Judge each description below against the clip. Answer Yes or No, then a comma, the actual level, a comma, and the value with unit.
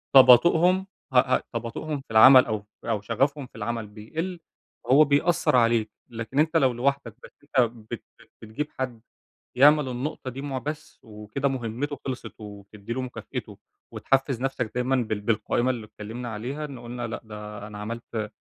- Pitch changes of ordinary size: Yes, average, 3.9 semitones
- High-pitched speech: No, low, 120 Hz